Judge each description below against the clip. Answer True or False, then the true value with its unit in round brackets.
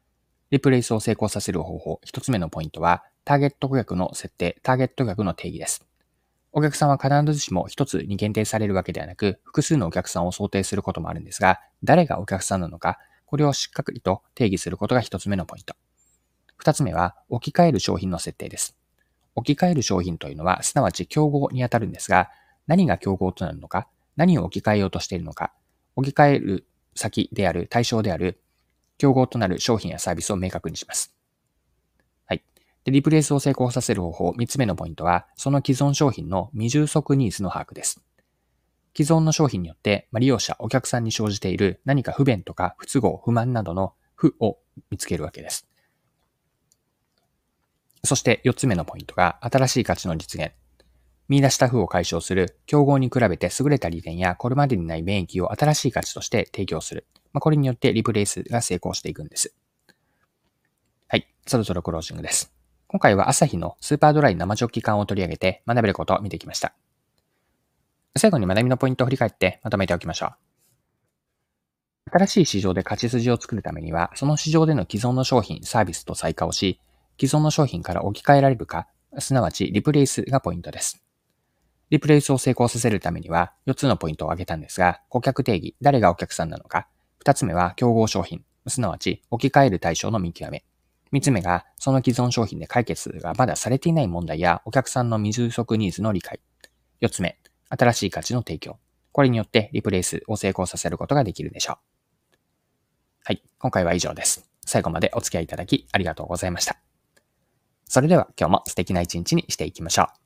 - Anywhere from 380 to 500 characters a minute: True (400 characters per minute)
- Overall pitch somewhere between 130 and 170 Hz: False (105 Hz)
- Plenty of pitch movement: True (6.8 semitones)